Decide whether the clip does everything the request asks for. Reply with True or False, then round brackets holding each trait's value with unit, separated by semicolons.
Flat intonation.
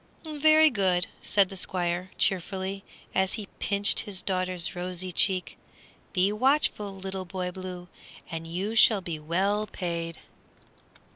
True (2.1 semitones)